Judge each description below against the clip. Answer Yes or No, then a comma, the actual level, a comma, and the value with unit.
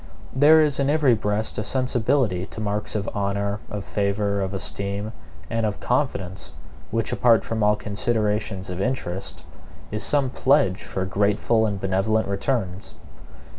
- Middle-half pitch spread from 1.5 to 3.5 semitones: Yes, average, 3.1 semitones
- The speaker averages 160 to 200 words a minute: No, average, 145 wpm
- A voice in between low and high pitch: No, low, 105 Hz